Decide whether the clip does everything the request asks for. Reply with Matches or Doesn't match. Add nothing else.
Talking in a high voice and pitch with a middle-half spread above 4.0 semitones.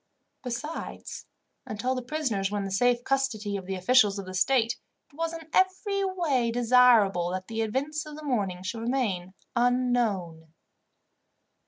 Matches